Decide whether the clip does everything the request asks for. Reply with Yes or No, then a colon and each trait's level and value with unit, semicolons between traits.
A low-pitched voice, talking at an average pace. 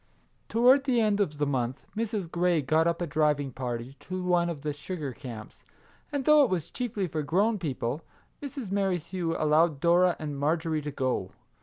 No: medium, 165 Hz; average, 180 wpm